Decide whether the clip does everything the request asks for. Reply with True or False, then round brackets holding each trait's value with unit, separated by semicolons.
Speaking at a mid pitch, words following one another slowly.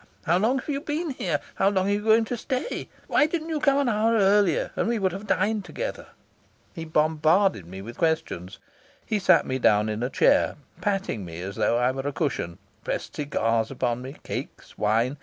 False (180 Hz; 205 wpm)